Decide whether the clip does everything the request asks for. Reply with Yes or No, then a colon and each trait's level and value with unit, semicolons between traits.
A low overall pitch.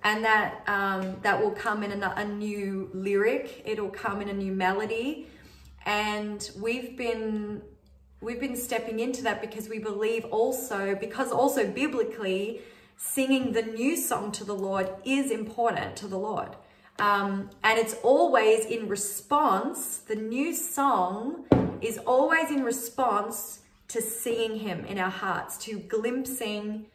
No: high, 220 Hz